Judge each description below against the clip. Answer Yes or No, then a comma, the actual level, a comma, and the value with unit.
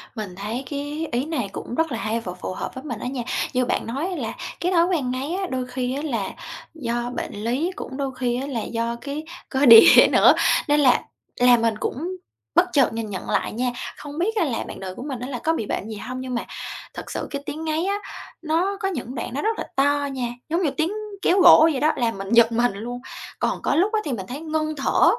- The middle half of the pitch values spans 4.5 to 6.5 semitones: Yes, average, 4.9 semitones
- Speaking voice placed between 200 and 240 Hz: No, very high, 265 Hz